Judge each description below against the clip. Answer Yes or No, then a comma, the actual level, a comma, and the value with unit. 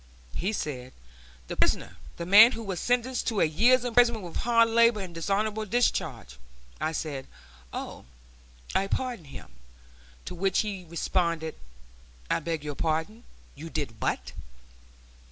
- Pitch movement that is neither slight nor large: No, wide, 6.1 semitones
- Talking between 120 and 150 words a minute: Yes, average, 140 wpm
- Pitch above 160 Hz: Yes, high, 190 Hz